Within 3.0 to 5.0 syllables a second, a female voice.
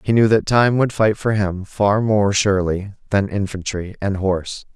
No: 4.6 syllables/s; male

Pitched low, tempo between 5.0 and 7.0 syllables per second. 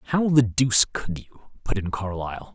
Yes: low, 110 Hz; 5.3 syllables/s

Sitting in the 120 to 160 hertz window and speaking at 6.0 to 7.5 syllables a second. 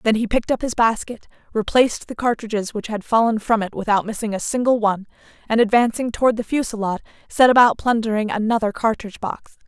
No: high, 225 Hz; 6.3 syllables/s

